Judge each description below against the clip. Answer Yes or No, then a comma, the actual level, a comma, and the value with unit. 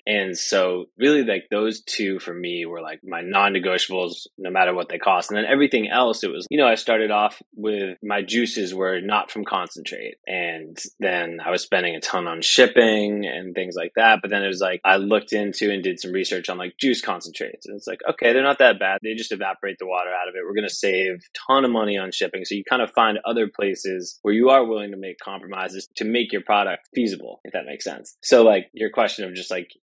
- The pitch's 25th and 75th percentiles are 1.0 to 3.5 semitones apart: Yes, average, 2.9 semitones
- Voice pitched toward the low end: Yes, low, 100 Hz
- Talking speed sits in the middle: No, fast, 240 wpm